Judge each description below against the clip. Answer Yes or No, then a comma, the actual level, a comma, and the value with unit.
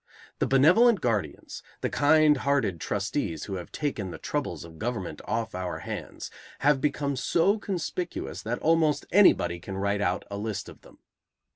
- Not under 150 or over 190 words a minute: Yes, average, 160 wpm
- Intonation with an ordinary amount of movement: No, wide, 7.6 semitones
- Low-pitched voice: Yes, low, 120 Hz